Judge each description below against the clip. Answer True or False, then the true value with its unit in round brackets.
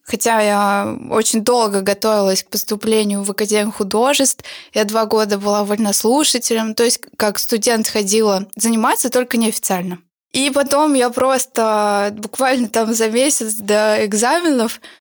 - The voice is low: False (225 Hz)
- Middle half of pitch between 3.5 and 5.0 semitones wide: False (2.7 semitones)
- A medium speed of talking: True (130 wpm)